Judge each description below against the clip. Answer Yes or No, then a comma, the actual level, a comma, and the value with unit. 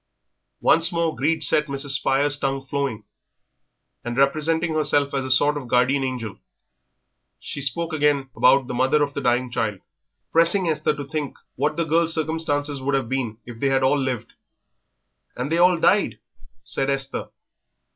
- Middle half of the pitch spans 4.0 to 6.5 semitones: No, average, 2.8 semitones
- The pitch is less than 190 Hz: Yes, medium, 140 Hz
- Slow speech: No, average, 165 wpm